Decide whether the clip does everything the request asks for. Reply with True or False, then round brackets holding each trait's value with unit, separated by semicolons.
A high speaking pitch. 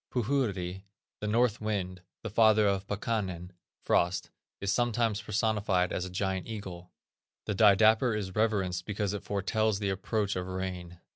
False (100 Hz)